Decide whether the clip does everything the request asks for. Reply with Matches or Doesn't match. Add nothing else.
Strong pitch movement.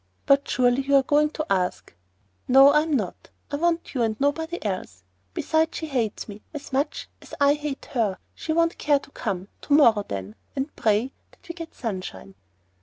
Matches